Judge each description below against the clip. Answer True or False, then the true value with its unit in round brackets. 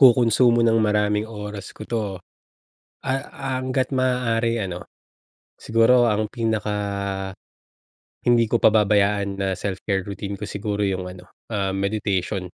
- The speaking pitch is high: False (105 Hz)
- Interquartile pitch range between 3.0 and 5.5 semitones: False (2.6 semitones)